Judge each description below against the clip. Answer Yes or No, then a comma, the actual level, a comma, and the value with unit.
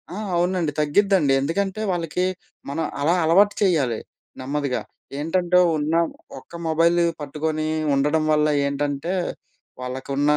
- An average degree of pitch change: Yes, average, 3.3 semitones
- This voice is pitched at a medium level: Yes, medium, 155 Hz